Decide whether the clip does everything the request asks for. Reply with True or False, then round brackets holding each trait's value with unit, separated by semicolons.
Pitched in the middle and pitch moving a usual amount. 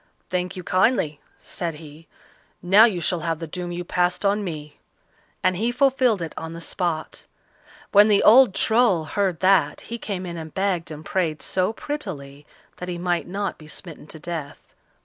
True (180 Hz; 3.6 semitones)